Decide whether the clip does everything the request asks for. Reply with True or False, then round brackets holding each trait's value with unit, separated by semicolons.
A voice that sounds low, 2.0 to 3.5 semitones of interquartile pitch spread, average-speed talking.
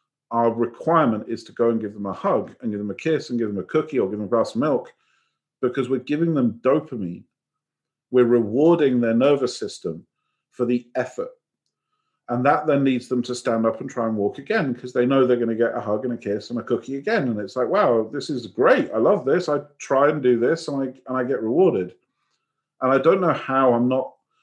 False (125 Hz; 2.8 semitones; 240 wpm)